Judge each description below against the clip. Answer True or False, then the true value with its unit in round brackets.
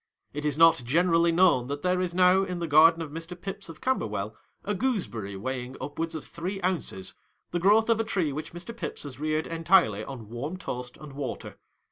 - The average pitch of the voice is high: False (165 Hz)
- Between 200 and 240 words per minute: True (205 wpm)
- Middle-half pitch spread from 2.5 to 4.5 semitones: False (5.2 semitones)